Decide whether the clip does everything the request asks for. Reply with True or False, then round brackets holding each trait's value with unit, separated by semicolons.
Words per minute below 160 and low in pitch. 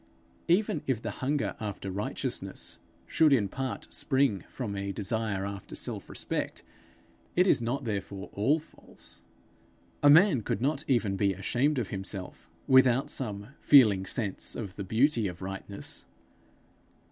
True (140 wpm; 110 Hz)